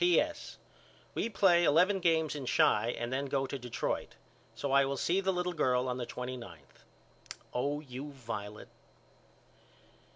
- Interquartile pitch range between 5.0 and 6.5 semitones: Yes, wide, 5.5 semitones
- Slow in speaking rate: No, average, 155 wpm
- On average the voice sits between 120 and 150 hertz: Yes, medium, 140 Hz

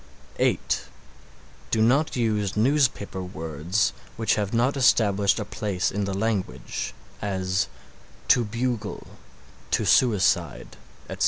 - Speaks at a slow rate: Yes, slow, 110 wpm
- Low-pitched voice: Yes, low, 105 Hz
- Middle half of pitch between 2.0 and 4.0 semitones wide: Yes, average, 3.5 semitones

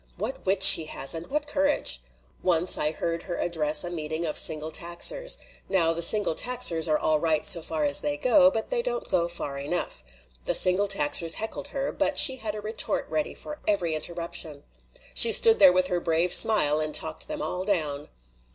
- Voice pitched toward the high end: No, medium, 175 Hz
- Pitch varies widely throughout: Yes, wide, 5.7 semitones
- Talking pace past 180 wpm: Yes, average, 195 wpm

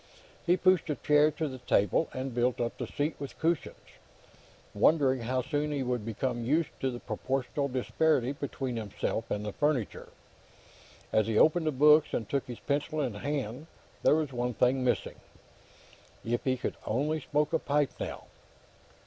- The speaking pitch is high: No, low, 135 Hz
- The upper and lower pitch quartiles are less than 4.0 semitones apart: Yes, average, 3.6 semitones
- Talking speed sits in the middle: Yes, average, 175 wpm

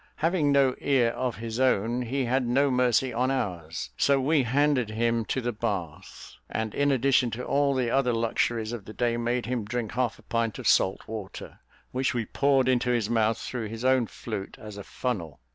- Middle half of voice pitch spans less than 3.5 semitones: Yes, average, 2.8 semitones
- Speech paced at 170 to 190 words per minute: No, average, 200 wpm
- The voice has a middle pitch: No, low, 120 Hz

